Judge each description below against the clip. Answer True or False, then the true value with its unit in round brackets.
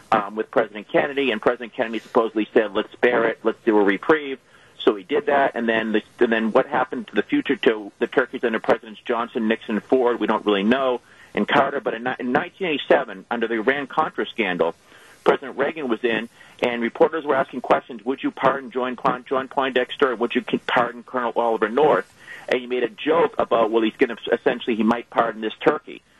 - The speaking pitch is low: True (120 Hz)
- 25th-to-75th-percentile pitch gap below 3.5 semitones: True (2.8 semitones)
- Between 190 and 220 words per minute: True (205 wpm)